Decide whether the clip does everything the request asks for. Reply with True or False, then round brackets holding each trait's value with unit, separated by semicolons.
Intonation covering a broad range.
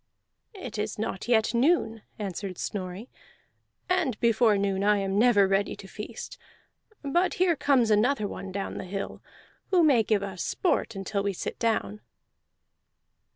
False (3.8 semitones)